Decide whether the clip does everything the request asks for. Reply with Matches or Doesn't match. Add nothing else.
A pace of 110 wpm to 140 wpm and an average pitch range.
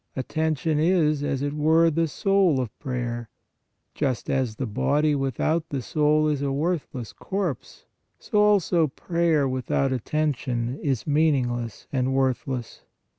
Matches